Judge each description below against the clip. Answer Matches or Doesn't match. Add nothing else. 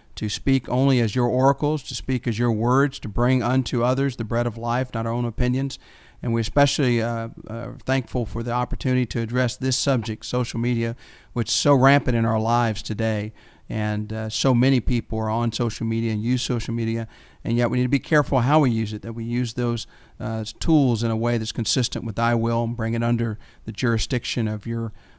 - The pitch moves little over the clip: Matches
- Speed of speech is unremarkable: Doesn't match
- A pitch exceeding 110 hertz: Matches